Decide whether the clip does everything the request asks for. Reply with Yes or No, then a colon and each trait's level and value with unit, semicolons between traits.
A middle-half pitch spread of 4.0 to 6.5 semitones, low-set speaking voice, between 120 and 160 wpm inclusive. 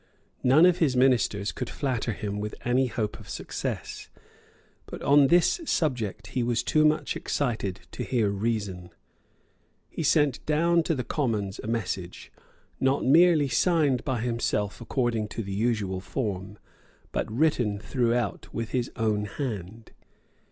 Yes: average, 4.8 semitones; low, 120 Hz; average, 145 wpm